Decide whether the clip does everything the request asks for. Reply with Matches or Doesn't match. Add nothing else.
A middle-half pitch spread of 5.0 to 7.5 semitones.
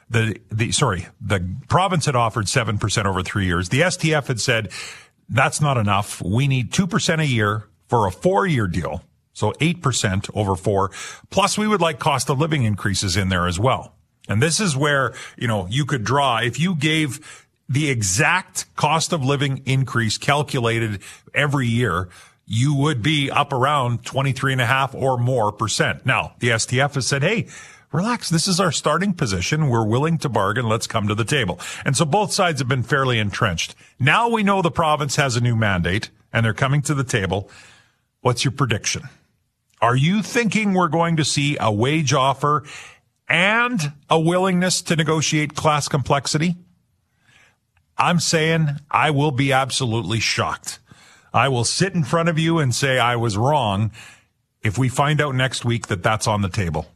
Matches